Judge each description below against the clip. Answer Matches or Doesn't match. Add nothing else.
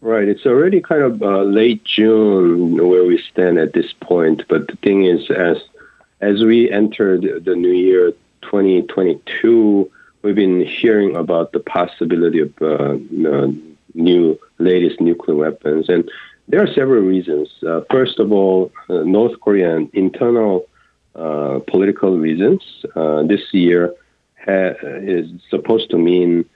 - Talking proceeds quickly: Doesn't match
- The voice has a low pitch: Matches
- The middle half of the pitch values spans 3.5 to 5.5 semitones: Matches